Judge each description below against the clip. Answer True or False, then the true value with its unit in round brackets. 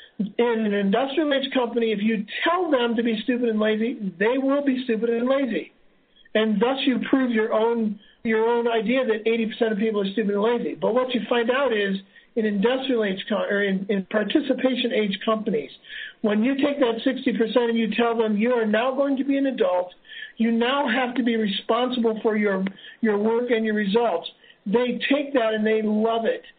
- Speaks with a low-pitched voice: False (230 Hz)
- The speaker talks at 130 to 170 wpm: False (200 wpm)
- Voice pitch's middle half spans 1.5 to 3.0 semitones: True (2.7 semitones)